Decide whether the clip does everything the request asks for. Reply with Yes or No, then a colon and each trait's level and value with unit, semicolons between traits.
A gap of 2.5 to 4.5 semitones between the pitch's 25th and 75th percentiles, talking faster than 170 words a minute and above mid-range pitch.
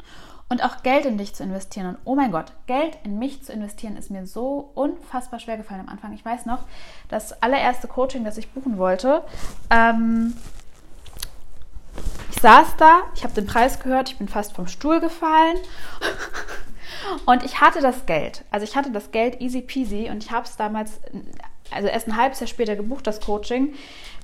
Yes: average, 4.0 semitones; average, 185 wpm; high, 245 Hz